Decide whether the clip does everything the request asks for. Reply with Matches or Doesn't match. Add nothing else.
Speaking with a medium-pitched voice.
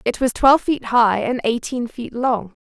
Doesn't match